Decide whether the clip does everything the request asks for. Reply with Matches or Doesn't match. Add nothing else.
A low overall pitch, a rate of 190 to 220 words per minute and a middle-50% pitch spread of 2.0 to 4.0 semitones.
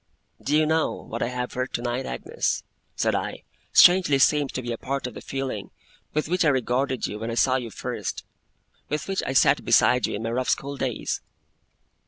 Matches